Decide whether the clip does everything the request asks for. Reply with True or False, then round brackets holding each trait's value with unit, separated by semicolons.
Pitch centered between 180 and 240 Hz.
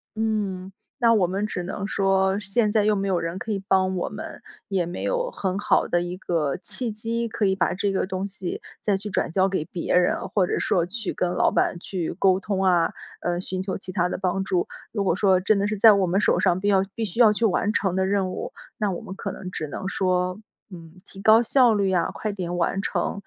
True (190 Hz)